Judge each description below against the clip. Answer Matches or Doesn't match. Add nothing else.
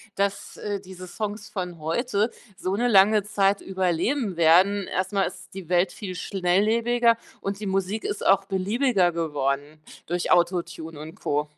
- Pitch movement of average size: Matches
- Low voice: Doesn't match